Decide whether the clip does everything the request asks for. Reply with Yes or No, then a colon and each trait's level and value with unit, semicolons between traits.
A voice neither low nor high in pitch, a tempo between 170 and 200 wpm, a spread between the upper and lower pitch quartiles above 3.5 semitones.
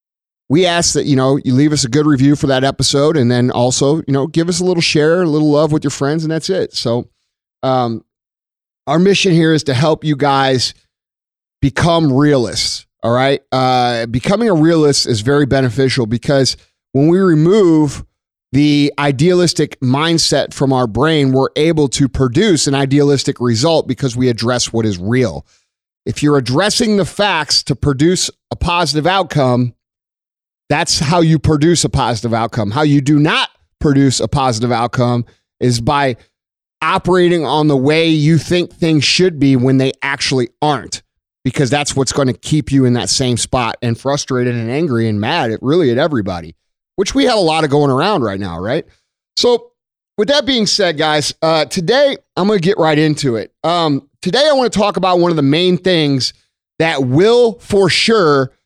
Yes: medium, 145 Hz; average, 185 wpm; average, 4.1 semitones